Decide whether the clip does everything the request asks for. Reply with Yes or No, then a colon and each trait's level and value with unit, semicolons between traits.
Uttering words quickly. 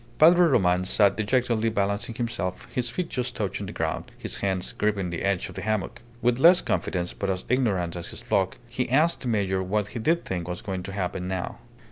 Yes: fast, 210 wpm